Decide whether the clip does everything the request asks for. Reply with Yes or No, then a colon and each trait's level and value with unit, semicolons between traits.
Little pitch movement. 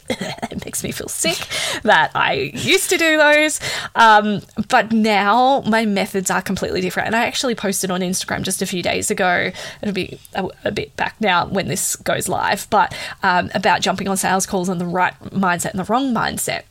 No: average, 3.7 semitones